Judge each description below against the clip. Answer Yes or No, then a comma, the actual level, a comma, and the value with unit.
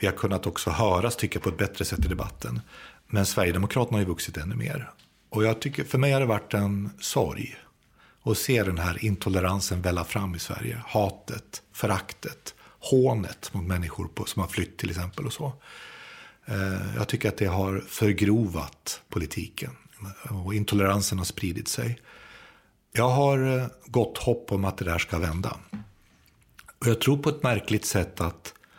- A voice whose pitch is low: Yes, low, 100 Hz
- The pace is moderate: Yes, average, 170 wpm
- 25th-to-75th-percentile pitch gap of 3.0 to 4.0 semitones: Yes, average, 3.5 semitones